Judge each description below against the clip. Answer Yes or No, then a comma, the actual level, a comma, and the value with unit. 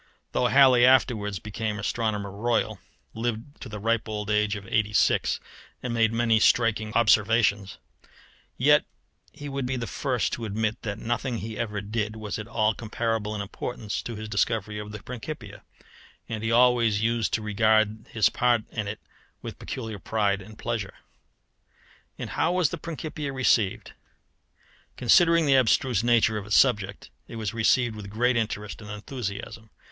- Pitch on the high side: No, low, 110 Hz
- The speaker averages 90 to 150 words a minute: No, average, 160 wpm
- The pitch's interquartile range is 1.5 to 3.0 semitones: Yes, narrow, 2.4 semitones